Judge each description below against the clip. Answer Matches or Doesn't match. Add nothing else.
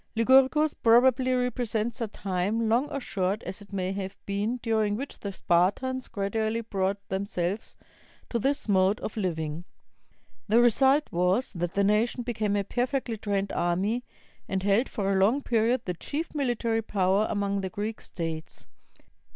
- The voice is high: Matches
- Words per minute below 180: Matches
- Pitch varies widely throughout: Doesn't match